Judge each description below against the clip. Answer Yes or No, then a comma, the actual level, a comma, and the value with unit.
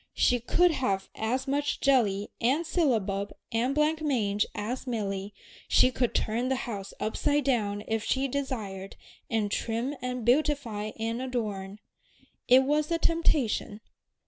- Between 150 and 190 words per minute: No, average, 140 wpm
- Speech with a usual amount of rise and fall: Yes, average, 4.7 semitones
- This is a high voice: Yes, high, 245 Hz